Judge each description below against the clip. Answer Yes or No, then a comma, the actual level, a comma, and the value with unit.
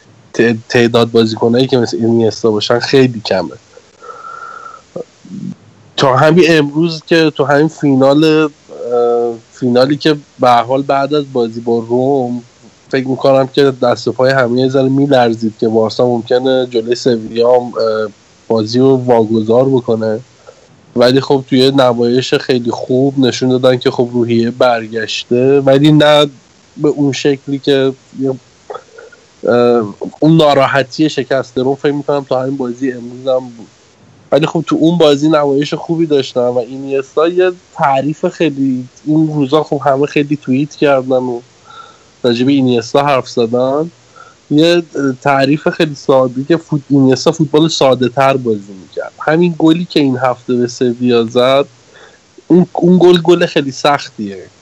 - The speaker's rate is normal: Yes, average, 135 wpm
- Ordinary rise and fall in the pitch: Yes, average, 3.5 semitones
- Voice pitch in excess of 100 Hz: Yes, low, 135 Hz